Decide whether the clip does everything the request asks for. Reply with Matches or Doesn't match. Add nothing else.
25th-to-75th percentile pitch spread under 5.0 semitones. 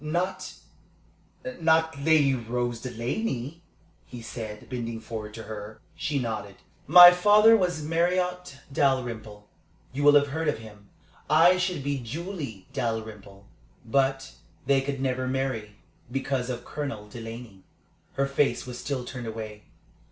Doesn't match